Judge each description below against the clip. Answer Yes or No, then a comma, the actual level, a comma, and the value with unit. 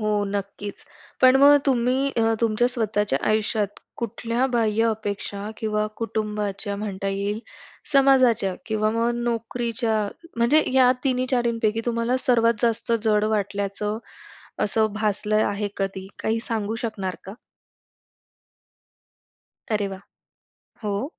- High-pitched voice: Yes, high, 220 Hz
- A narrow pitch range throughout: Yes, narrow, 2.3 semitones